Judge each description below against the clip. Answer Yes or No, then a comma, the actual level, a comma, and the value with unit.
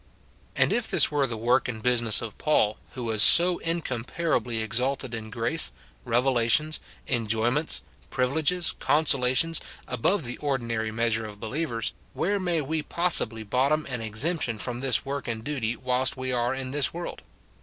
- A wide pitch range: No, average, 4.8 semitones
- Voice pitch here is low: Yes, low, 125 Hz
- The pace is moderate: Yes, average, 155 wpm